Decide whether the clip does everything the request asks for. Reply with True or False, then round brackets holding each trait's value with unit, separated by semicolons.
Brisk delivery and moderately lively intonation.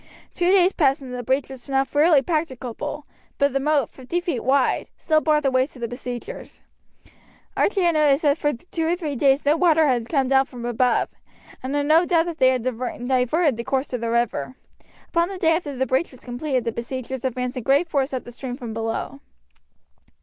True (210 wpm; 3.6 semitones)